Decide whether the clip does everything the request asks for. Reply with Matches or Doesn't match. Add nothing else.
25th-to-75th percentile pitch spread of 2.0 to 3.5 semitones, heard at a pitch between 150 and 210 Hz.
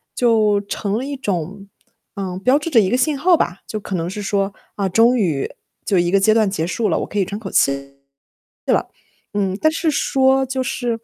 Doesn't match